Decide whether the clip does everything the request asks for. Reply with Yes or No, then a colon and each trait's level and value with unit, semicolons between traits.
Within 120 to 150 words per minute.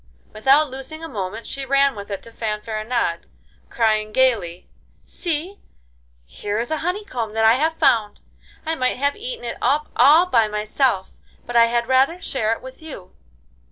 No: average, 165 wpm